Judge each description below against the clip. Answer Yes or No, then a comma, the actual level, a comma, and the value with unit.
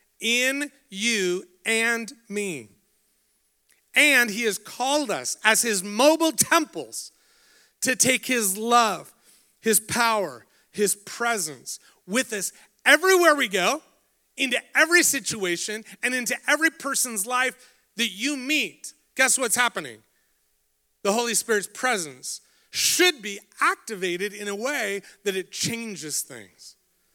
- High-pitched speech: Yes, high, 230 Hz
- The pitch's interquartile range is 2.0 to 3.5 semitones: No, average, 4.5 semitones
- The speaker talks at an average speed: No, slow, 120 wpm